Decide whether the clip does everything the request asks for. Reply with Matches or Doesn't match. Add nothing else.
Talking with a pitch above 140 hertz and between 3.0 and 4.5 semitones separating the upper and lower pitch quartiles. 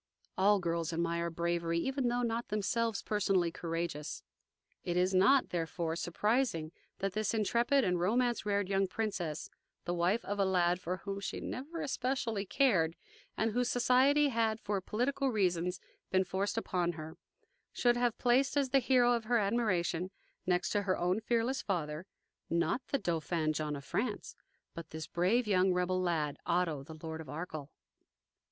Doesn't match